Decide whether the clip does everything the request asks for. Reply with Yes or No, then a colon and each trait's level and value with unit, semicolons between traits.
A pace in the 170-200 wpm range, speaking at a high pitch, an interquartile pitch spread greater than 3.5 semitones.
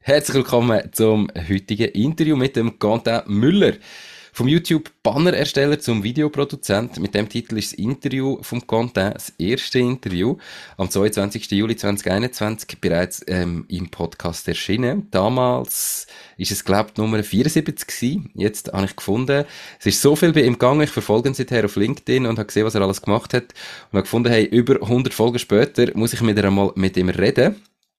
No: average, 175 wpm; low, 115 Hz; average, 4.4 semitones